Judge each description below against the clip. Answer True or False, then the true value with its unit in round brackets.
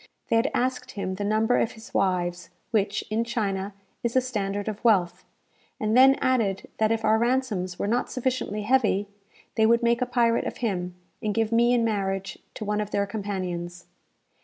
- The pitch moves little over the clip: False (3.1 semitones)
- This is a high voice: True (215 Hz)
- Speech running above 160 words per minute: True (185 wpm)